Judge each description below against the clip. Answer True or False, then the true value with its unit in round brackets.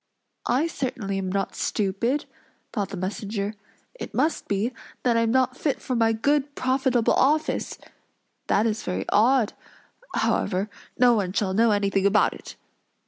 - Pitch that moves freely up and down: False (4.4 semitones)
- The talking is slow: False (150 wpm)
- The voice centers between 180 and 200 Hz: False (225 Hz)